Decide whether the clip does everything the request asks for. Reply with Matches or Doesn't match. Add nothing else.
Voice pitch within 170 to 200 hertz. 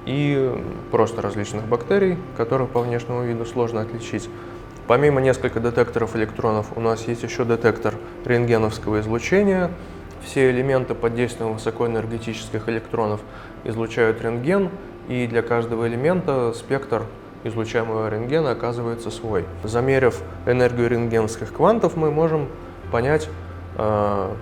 Doesn't match